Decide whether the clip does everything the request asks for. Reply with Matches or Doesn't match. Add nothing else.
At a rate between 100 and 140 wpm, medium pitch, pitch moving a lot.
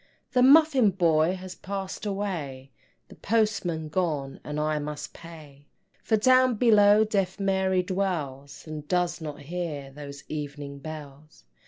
Doesn't match